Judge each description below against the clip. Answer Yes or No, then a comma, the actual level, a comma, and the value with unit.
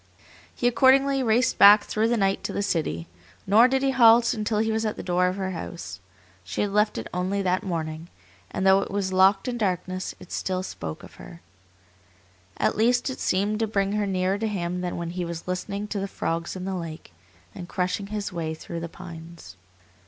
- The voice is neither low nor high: No, high, 195 Hz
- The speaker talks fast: Yes, fast, 210 wpm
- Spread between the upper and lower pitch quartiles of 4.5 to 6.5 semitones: No, average, 3.4 semitones